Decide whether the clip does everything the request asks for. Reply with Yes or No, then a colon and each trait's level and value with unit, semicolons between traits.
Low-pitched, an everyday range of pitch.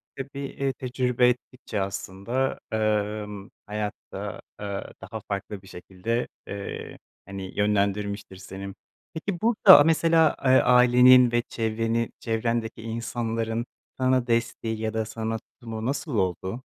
Yes: low, 115 Hz; average, 3.3 semitones